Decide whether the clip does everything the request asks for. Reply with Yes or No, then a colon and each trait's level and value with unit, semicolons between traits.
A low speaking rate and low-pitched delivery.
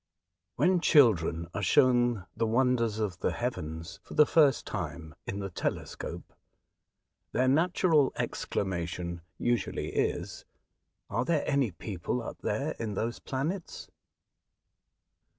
Yes: slow, 120 wpm; low, 115 Hz